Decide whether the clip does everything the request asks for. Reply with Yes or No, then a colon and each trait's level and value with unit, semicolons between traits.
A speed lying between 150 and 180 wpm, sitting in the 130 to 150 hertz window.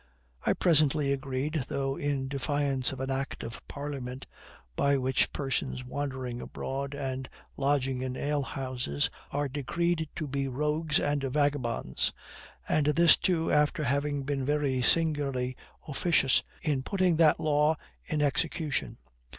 No: slow, 135 wpm; medium, 140 Hz